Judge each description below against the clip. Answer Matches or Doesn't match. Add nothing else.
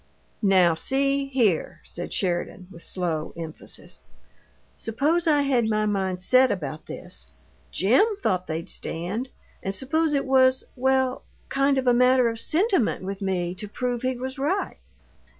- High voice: Matches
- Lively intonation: Matches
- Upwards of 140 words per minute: Matches